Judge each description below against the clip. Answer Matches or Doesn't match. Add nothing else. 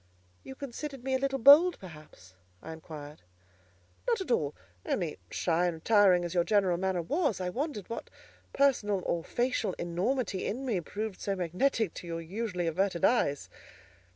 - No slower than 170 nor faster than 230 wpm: Doesn't match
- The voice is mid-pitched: Doesn't match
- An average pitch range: Doesn't match